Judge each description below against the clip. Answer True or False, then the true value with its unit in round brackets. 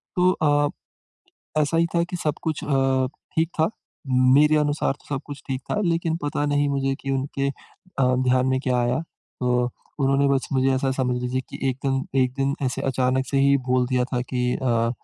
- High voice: False (135 Hz)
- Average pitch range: False (2.3 semitones)